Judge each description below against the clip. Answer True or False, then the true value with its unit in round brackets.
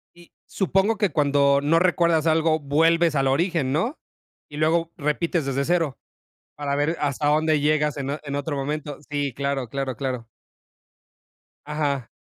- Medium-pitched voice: True (150 Hz)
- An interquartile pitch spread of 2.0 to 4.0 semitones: True (2.8 semitones)